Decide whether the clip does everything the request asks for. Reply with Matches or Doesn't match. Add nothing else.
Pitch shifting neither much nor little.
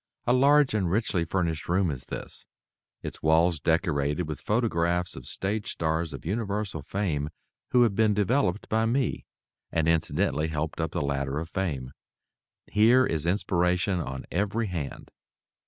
Matches